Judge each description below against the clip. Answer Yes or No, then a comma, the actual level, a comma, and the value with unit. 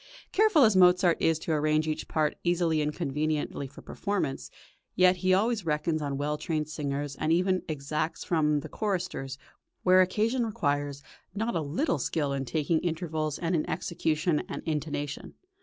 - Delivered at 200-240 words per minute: No, average, 160 wpm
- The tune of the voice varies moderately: Yes, average, 3.5 semitones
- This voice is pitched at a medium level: Yes, medium, 155 Hz